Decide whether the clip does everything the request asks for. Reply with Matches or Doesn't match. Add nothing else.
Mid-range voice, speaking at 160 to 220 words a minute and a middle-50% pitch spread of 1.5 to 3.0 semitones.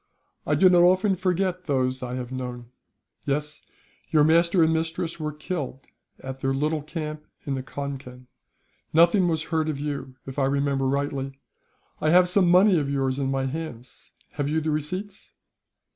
Doesn't match